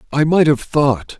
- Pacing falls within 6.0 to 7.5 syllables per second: No, 4.3 syllables/s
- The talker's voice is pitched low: No, medium, 145 Hz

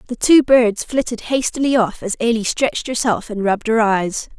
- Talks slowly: No, average, 190 wpm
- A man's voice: No, female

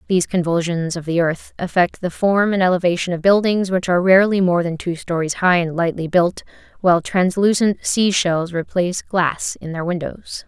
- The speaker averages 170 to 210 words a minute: Yes, average, 185 wpm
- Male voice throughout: No, female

